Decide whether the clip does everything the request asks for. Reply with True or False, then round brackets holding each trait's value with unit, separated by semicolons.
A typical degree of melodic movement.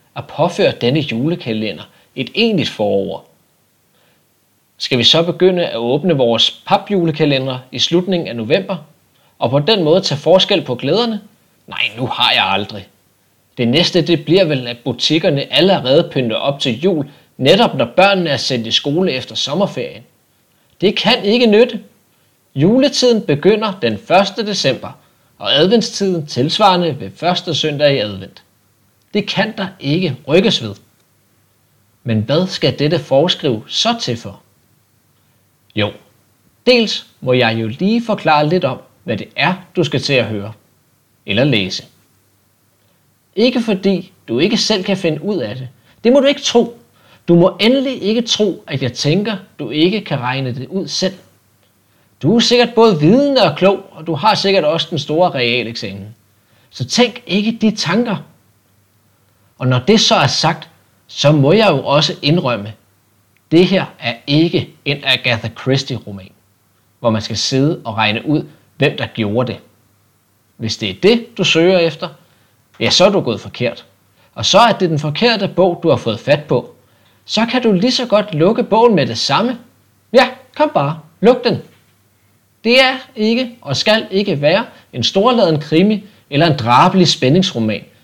False (9.0 semitones)